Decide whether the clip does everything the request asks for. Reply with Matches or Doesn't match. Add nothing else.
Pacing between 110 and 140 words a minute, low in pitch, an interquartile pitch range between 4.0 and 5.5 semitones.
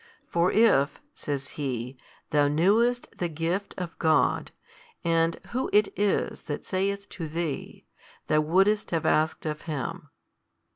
Doesn't match